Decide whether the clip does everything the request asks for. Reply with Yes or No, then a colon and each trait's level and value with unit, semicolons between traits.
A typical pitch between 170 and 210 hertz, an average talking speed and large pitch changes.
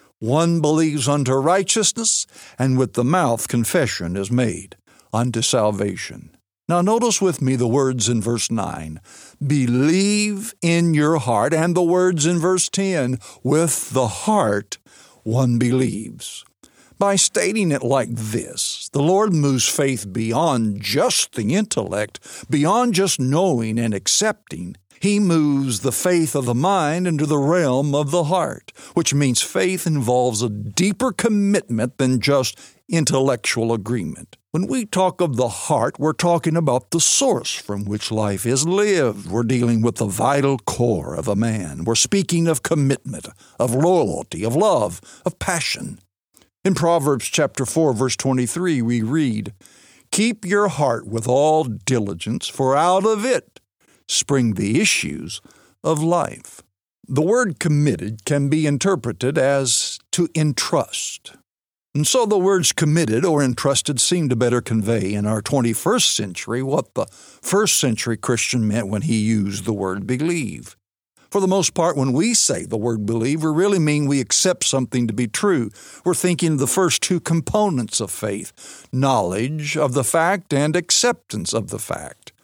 No: medium, 140 Hz; average, 155 wpm; wide, 6.5 semitones